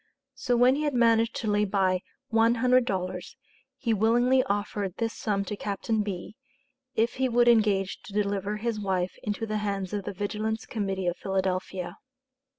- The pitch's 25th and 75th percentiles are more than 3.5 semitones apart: No, average, 2.9 semitones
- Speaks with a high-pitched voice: Yes, high, 210 Hz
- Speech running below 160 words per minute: No, average, 170 wpm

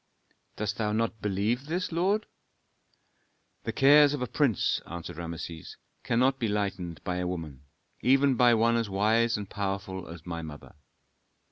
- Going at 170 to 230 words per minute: No, average, 150 wpm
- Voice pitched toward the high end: No, low, 105 Hz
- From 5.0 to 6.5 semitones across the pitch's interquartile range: Yes, wide, 5.6 semitones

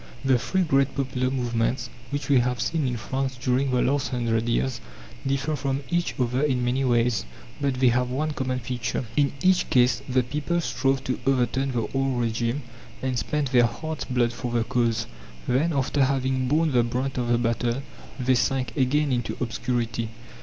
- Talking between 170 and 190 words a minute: Yes, average, 180 wpm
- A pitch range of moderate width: No, narrow, 2.0 semitones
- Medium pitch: No, low, 130 Hz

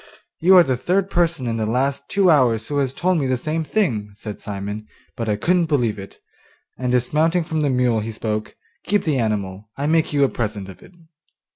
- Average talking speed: No, fast, 215 wpm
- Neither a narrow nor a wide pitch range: No, wide, 6.9 semitones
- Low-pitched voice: Yes, low, 130 Hz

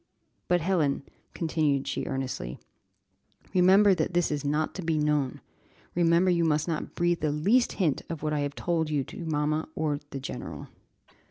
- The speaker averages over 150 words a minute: Yes, average, 170 wpm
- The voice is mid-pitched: Yes, medium, 155 Hz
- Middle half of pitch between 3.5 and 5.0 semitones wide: No, average, 3.0 semitones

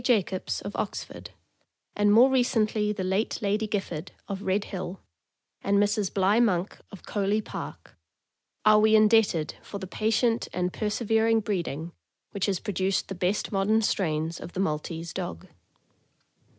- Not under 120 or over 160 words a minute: Yes, average, 150 wpm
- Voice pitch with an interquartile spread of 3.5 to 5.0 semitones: No, average, 2.7 semitones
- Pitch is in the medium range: No, high, 200 Hz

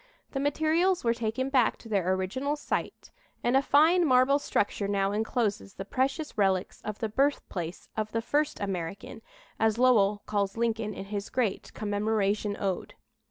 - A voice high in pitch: Yes, high, 220 Hz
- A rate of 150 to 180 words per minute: Yes, average, 160 wpm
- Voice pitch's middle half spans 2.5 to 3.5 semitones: No, average, 4.8 semitones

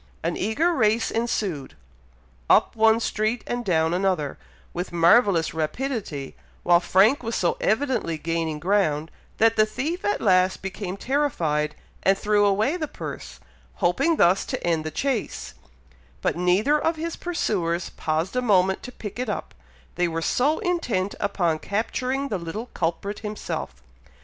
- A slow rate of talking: No, average, 150 wpm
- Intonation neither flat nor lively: No, wide, 6.1 semitones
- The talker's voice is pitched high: Yes, high, 200 Hz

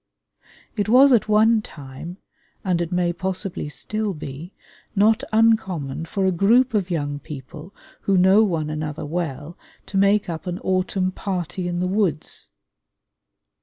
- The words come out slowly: No, average, 145 wpm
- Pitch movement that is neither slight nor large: Yes, average, 4.3 semitones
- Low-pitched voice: No, medium, 180 Hz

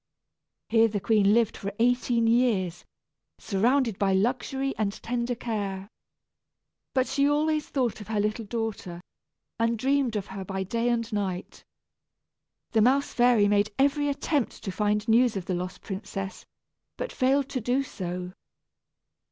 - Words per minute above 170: No, average, 145 wpm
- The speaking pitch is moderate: No, high, 225 Hz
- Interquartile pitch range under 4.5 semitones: Yes, average, 4.0 semitones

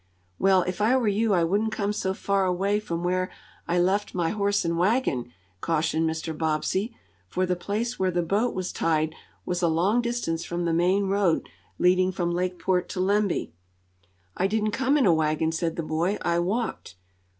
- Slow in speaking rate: No, average, 185 wpm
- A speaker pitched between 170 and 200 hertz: Yes, medium, 185 Hz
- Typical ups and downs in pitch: Yes, average, 3.4 semitones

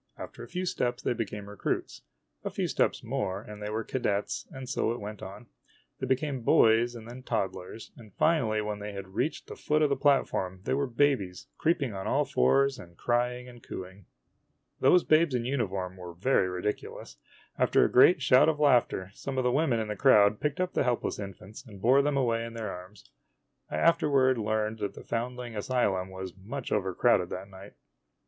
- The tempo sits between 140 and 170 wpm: No, average, 195 wpm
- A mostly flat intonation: No, average, 4.7 semitones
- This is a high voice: No, low, 115 Hz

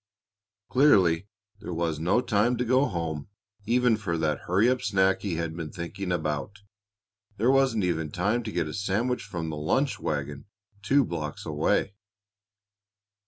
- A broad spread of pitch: Yes, wide, 5.9 semitones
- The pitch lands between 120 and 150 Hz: No, very low, 95 Hz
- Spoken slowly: No, average, 155 wpm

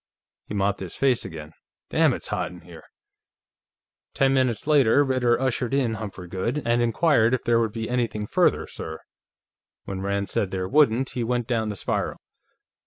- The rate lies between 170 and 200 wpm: Yes, average, 175 wpm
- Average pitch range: Yes, average, 4.5 semitones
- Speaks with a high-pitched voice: No, low, 115 Hz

